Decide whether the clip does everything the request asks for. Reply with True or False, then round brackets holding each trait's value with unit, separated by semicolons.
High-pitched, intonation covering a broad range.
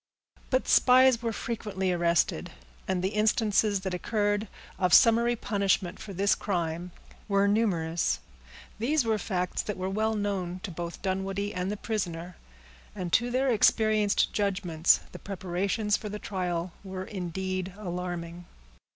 False (195 Hz; 3.0 semitones)